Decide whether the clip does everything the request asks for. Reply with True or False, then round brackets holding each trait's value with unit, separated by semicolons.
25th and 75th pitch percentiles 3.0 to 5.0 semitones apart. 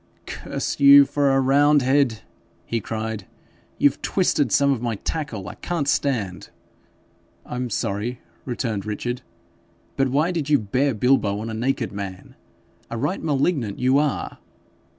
True (4.3 semitones)